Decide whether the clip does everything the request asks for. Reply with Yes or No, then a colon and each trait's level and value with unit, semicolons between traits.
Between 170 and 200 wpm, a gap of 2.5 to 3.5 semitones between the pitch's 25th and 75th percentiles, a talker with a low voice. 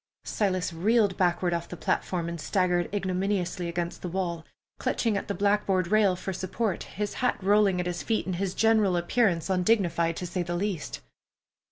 No: average, 175 wpm; average, 2.8 semitones; medium, 185 Hz